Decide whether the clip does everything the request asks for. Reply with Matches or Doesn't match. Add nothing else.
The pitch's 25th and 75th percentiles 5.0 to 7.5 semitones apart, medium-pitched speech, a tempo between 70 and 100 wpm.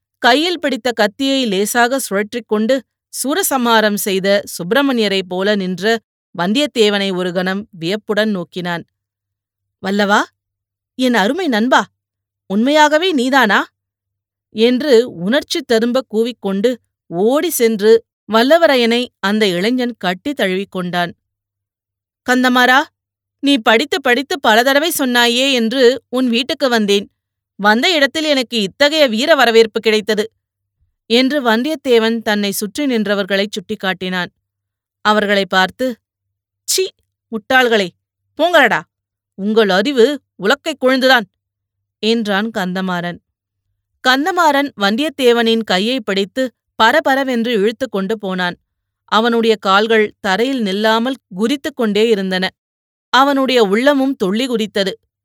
Doesn't match